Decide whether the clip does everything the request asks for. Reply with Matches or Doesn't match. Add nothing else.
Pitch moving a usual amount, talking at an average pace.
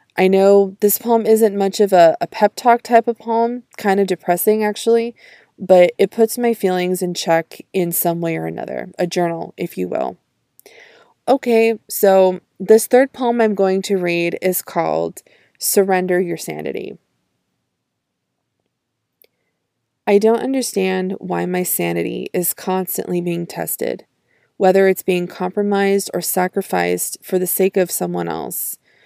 Matches